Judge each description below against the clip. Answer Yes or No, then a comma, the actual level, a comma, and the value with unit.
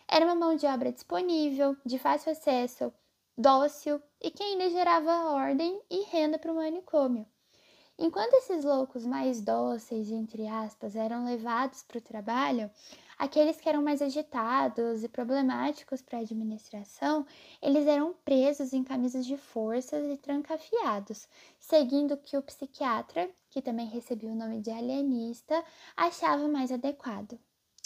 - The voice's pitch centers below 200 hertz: No, very high, 280 Hz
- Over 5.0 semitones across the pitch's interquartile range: No, average, 4.5 semitones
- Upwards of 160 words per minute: No, average, 140 wpm